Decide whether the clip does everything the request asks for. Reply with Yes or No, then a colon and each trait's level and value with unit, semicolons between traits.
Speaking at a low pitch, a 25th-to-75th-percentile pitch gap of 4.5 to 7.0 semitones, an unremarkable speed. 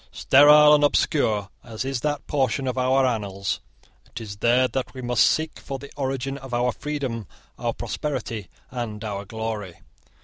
No: low, 125 Hz; average, 3.7 semitones; average, 165 wpm